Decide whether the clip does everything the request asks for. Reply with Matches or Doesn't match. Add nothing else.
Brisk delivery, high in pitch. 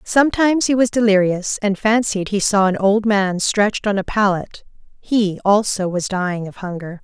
Doesn't match